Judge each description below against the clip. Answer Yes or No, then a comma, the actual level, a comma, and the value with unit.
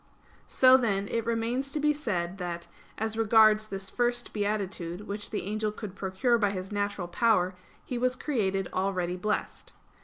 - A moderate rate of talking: Yes, average, 160 wpm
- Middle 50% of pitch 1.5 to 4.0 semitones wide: Yes, average, 3.4 semitones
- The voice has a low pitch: No, high, 210 Hz